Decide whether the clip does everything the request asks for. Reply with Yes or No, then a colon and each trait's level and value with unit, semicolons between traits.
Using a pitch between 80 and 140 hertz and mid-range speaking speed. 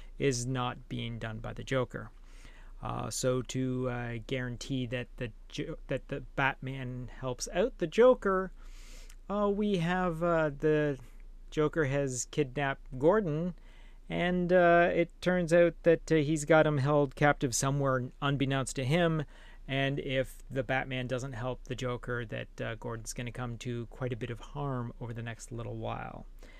Yes: low, 135 Hz; average, 160 wpm